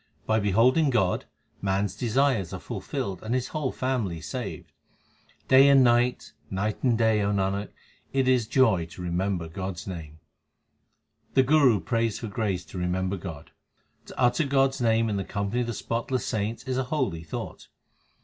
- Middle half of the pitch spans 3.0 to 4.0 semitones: No, average, 5.0 semitones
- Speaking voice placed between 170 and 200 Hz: No, low, 110 Hz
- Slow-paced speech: No, average, 175 wpm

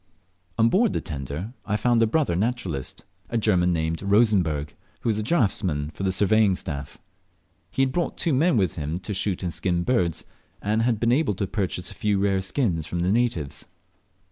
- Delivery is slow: No, average, 190 wpm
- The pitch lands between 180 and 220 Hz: No, low, 100 Hz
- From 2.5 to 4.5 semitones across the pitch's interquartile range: No, average, 5.0 semitones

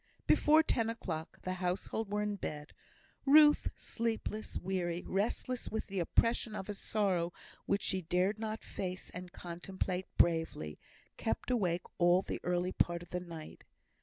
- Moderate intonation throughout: Yes, average, 3.7 semitones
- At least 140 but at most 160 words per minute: Yes, average, 150 wpm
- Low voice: No, medium, 185 Hz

